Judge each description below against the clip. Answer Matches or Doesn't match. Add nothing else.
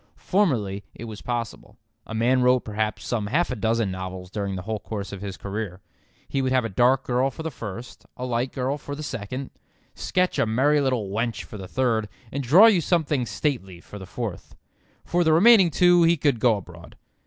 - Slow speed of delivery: Doesn't match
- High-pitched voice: Doesn't match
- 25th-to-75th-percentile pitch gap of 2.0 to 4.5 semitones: Doesn't match